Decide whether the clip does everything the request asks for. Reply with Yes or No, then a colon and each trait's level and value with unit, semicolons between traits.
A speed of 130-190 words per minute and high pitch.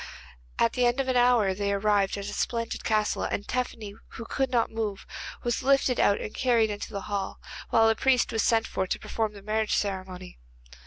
No: fast, 205 wpm; high, 220 Hz